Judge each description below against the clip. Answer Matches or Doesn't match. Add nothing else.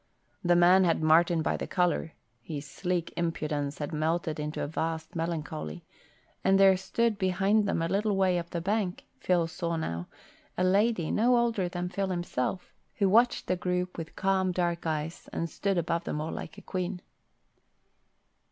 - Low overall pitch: Doesn't match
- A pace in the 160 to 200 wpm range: Matches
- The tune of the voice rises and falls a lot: Doesn't match